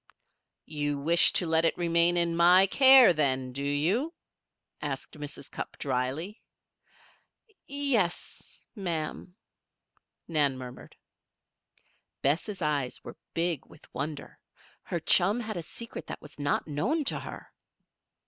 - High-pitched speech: No, medium, 165 Hz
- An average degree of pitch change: Yes, average, 4.8 semitones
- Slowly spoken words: Yes, slow, 125 wpm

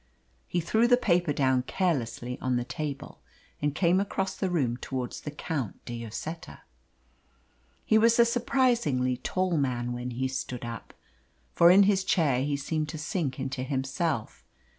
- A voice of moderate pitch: Yes, medium, 145 Hz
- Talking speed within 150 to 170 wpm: Yes, average, 160 wpm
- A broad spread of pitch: Yes, wide, 6.4 semitones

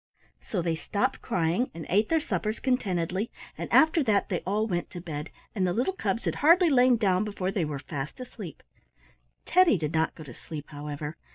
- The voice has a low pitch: No, high, 190 Hz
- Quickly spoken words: No, average, 195 wpm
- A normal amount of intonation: No, wide, 6.8 semitones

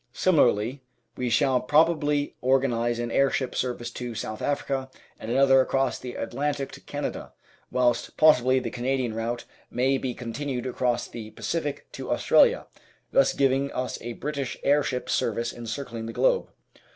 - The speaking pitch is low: Yes, low, 130 Hz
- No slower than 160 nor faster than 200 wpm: No, average, 145 wpm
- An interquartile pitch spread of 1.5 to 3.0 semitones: Yes, narrow, 2.6 semitones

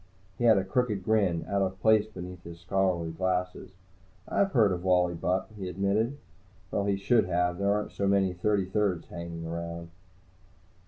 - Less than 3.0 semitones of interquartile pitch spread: Yes, narrow, 2.5 semitones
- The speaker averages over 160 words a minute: Yes, average, 170 wpm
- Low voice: Yes, very low, 95 Hz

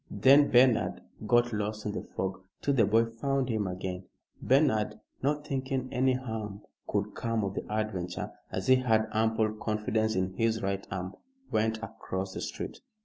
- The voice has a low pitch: Yes, low, 110 Hz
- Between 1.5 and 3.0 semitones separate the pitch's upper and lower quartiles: No, average, 3.6 semitones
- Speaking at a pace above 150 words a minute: Yes, average, 165 wpm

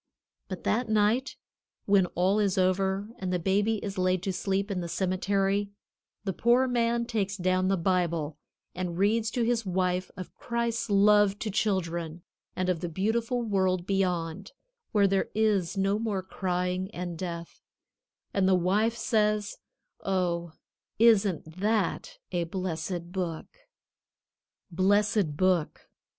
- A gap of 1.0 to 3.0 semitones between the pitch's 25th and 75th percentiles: Yes, narrow, 2.6 semitones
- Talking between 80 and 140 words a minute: Yes, slow, 135 wpm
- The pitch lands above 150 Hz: Yes, high, 190 Hz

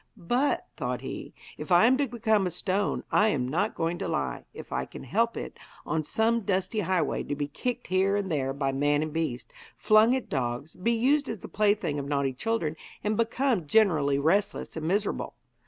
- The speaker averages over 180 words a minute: Yes, average, 200 wpm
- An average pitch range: No, wide, 7.0 semitones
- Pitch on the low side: No, medium, 185 Hz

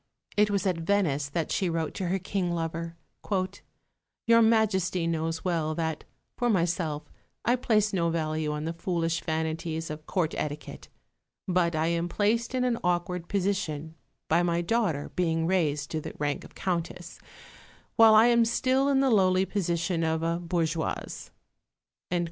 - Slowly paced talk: No, average, 155 wpm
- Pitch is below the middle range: No, medium, 170 Hz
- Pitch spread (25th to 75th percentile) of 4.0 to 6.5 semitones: No, average, 3.5 semitones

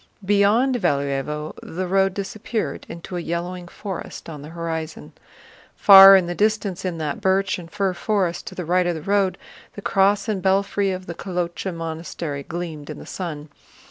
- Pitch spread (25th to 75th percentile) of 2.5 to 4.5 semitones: Yes, average, 2.9 semitones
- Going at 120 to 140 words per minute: No, average, 175 wpm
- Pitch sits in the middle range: Yes, medium, 180 Hz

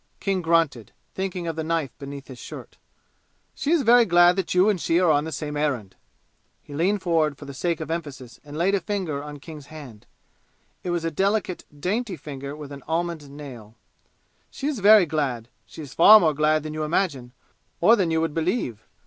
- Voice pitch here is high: No, medium, 160 Hz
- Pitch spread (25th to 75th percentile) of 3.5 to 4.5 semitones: Yes, average, 4.1 semitones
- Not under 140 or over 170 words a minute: No, average, 200 wpm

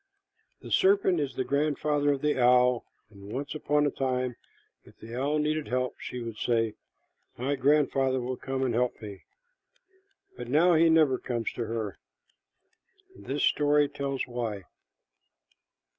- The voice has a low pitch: Yes, low, 130 Hz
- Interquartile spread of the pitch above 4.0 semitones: No, average, 3.3 semitones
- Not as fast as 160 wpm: Yes, average, 145 wpm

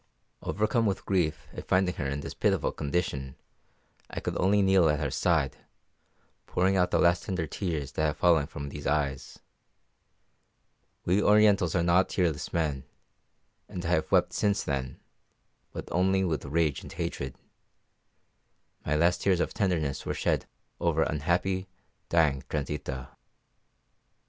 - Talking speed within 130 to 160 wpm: Yes, average, 145 wpm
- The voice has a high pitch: No, very low, 85 Hz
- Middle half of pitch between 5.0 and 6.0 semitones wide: No, average, 4.2 semitones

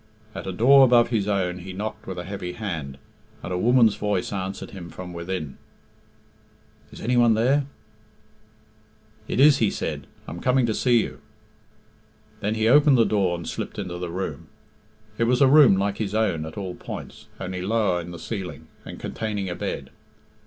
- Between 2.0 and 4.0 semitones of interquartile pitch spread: No, average, 4.5 semitones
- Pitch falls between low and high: No, low, 100 Hz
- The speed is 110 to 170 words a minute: No, average, 185 wpm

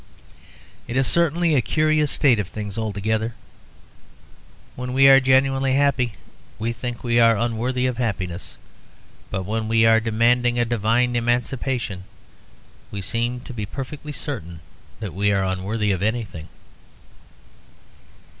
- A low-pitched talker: Yes, low, 115 Hz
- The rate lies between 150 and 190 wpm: No, slow, 135 wpm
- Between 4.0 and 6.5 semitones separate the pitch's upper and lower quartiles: No, average, 3.4 semitones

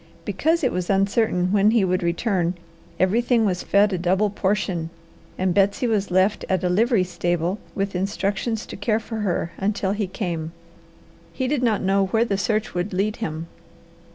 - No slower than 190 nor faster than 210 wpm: No, average, 175 wpm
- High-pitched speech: Yes, high, 195 Hz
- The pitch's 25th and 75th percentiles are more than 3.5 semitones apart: No, average, 2.9 semitones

